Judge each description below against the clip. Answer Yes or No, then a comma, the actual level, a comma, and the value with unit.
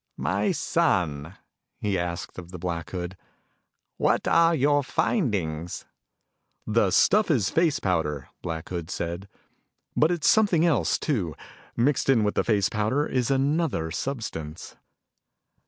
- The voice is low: Yes, low, 105 Hz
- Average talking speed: No, slow, 130 wpm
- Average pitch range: No, wide, 9.0 semitones